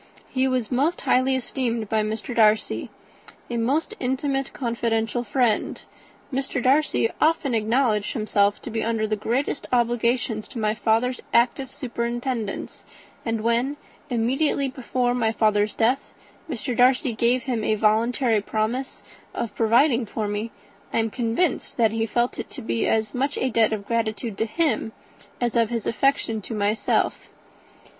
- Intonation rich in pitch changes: No, average, 2.8 semitones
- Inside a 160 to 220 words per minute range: No, average, 150 wpm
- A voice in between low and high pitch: No, high, 235 Hz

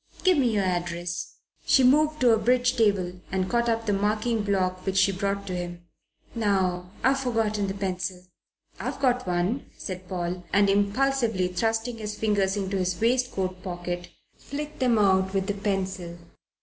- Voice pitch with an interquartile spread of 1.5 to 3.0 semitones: No, average, 4.0 semitones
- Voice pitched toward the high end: Yes, high, 200 Hz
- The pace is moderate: Yes, average, 165 wpm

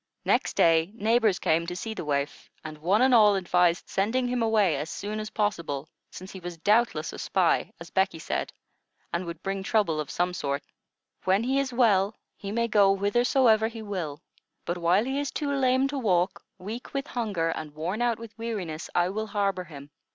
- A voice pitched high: Yes, high, 195 Hz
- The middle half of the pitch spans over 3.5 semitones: Yes, average, 5.0 semitones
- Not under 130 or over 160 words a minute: No, average, 195 wpm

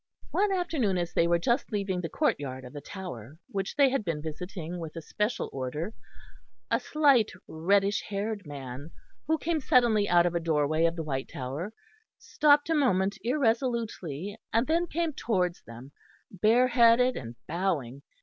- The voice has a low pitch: No, high, 190 Hz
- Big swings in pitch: Yes, wide, 7.2 semitones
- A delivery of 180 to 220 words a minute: No, average, 165 wpm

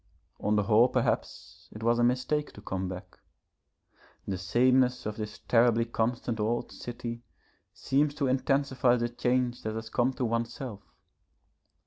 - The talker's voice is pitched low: Yes, low, 120 Hz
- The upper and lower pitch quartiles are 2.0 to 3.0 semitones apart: Yes, narrow, 2.5 semitones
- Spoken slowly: No, average, 145 wpm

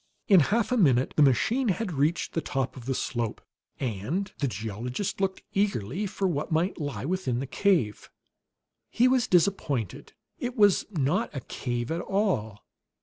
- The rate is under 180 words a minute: Yes, average, 160 wpm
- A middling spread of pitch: No, wide, 7.8 semitones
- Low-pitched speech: No, medium, 160 Hz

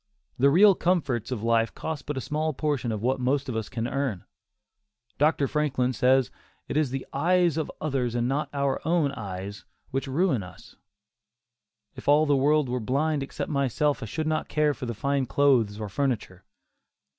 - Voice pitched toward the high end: No, low, 135 Hz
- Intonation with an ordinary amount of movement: Yes, average, 3.7 semitones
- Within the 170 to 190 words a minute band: Yes, average, 180 wpm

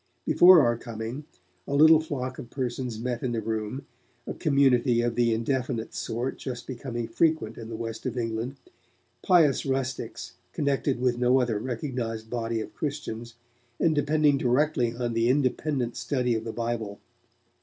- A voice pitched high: No, low, 125 Hz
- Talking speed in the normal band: Yes, average, 160 wpm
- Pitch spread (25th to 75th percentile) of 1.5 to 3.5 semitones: Yes, average, 3.1 semitones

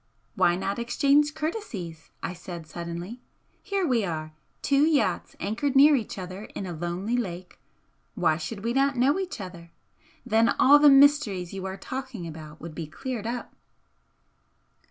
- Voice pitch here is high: Yes, high, 215 Hz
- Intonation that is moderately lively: No, wide, 7.9 semitones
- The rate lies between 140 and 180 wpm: Yes, average, 155 wpm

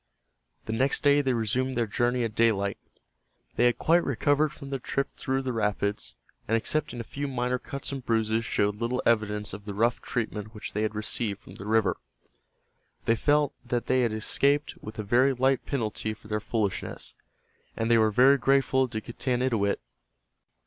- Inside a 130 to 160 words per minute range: No, average, 180 wpm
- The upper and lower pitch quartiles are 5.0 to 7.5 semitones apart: No, average, 3.5 semitones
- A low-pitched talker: Yes, low, 120 Hz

